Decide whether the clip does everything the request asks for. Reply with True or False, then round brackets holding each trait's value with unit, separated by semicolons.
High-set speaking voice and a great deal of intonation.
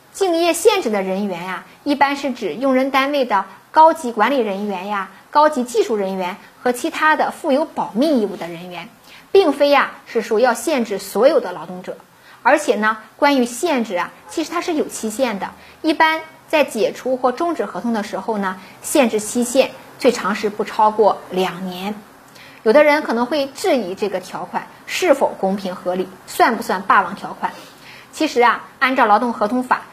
True (240 Hz; 6.7 semitones)